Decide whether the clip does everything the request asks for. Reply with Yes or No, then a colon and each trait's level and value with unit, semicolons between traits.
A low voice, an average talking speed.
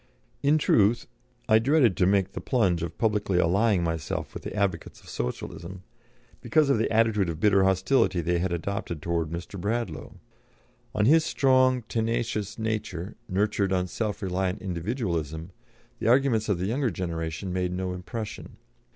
Yes: low, 100 Hz; average, 155 wpm